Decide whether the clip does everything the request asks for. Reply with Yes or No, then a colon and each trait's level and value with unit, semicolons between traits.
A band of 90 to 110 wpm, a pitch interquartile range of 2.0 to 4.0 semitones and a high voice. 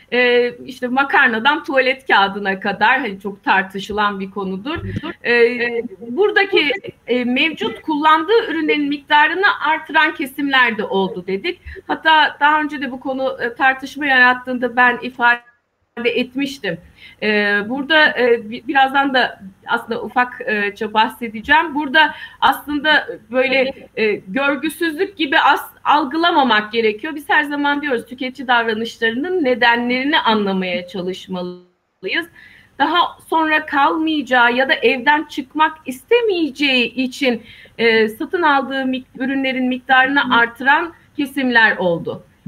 No: average, 100 wpm; average, 4.4 semitones; very high, 260 Hz